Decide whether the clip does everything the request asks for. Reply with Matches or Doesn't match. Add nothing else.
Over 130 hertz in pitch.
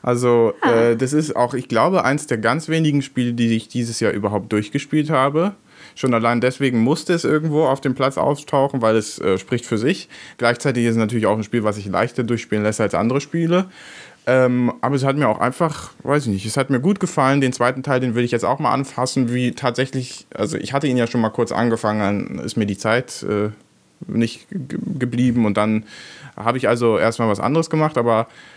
Doesn't match